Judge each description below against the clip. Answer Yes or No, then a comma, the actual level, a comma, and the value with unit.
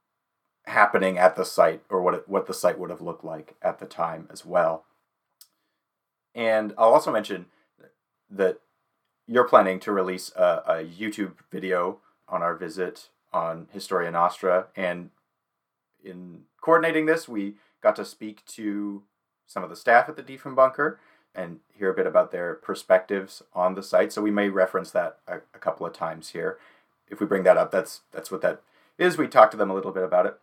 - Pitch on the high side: No, low, 100 Hz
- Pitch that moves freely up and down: Yes, wide, 6.1 semitones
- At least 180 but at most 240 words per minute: Yes, average, 185 wpm